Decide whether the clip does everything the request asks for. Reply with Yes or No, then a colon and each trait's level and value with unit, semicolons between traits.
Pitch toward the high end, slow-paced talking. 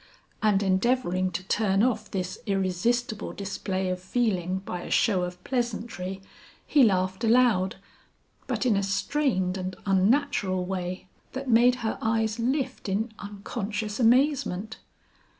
Yes: high, 205 Hz; slow, 130 wpm